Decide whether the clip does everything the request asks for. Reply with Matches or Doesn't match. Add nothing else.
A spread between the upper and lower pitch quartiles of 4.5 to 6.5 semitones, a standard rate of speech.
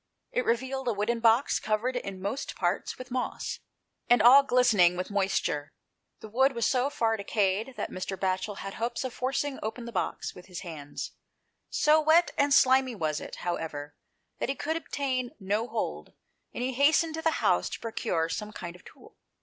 Matches